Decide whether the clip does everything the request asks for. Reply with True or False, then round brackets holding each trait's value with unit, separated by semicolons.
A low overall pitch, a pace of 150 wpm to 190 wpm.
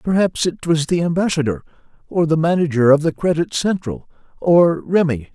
False (160 Hz; 155 wpm)